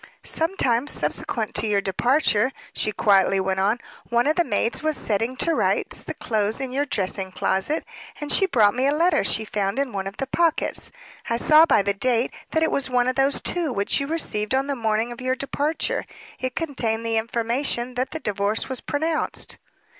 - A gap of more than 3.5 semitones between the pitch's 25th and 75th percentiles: Yes, average, 5.2 semitones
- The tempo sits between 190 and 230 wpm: Yes, average, 200 wpm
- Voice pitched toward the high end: Yes, high, 245 Hz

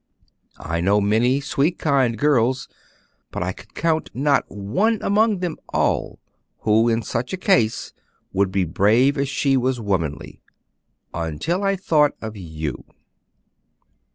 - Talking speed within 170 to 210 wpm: No, slow, 135 wpm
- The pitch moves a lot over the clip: Yes, wide, 6.8 semitones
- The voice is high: No, low, 125 Hz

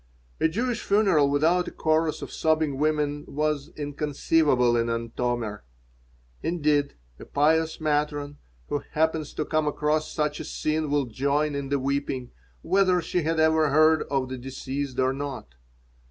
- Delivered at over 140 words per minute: Yes, average, 150 wpm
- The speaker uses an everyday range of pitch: No, narrow, 2.2 semitones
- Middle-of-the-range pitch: Yes, medium, 150 Hz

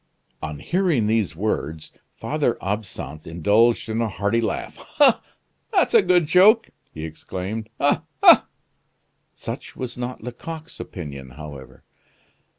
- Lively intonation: Yes, wide, 8.2 semitones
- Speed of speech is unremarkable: No, slow, 125 wpm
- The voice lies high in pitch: No, low, 110 Hz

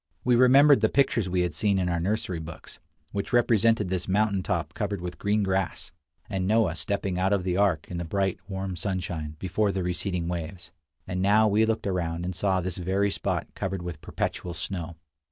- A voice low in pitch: Yes, very low, 95 Hz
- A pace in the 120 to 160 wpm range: No, average, 195 wpm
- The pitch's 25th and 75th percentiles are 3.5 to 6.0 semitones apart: No, narrow, 2.6 semitones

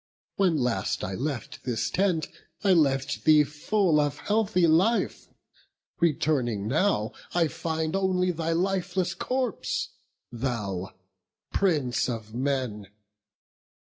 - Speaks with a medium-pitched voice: Yes, medium, 155 Hz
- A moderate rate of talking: No, slow, 110 wpm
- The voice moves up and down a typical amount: No, wide, 6.6 semitones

